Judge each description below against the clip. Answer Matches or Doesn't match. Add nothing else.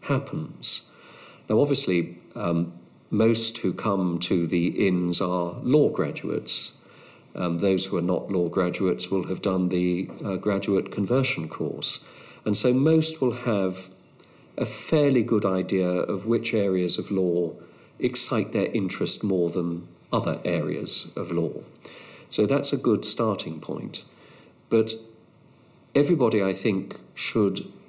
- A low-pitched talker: Matches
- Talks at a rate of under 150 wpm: Matches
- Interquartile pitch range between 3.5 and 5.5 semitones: Matches